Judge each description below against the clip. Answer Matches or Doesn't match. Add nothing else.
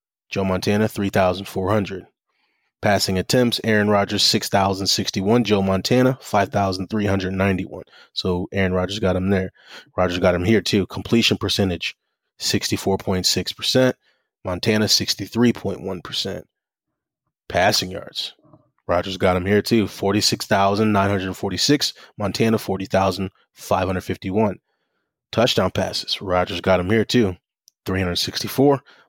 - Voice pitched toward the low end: Matches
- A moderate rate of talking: Doesn't match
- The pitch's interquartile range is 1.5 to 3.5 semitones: Matches